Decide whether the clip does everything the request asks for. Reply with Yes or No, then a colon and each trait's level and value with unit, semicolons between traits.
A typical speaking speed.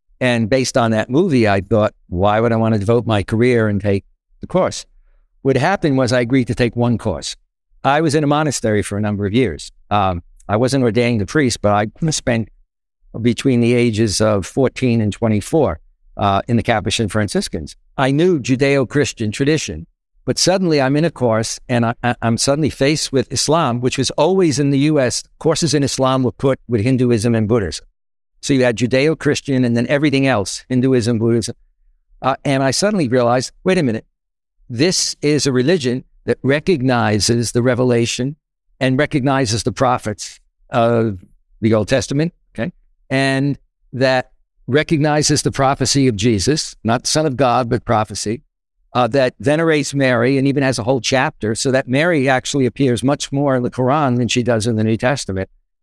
Yes: average, 175 wpm